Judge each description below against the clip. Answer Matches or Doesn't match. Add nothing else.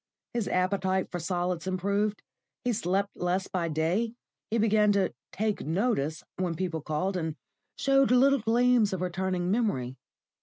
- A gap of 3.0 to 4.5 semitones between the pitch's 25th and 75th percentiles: Matches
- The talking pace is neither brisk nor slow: Matches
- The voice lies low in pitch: Doesn't match